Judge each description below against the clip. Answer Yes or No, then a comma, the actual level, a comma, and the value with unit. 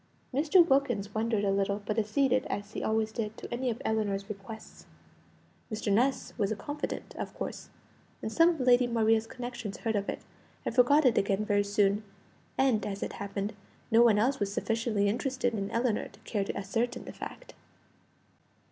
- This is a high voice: Yes, high, 220 Hz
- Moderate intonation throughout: Yes, average, 3.4 semitones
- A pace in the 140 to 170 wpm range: No, average, 180 wpm